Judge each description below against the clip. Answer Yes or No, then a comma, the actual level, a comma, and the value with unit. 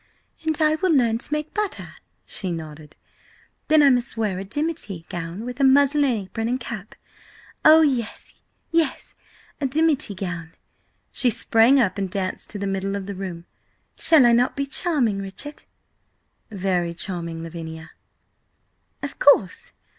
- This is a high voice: Yes, high, 225 Hz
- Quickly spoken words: No, average, 145 wpm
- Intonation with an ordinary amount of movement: No, wide, 7.3 semitones